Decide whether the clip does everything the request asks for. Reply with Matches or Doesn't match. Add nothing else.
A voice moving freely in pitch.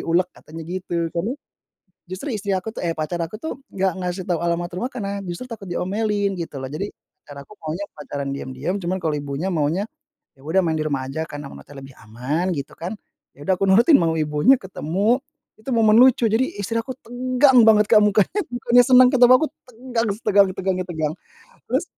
Matches